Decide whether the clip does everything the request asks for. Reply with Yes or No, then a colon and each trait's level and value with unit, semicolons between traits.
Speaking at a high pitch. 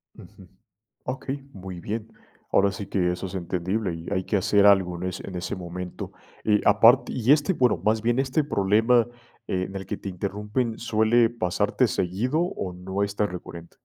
No: low, 100 Hz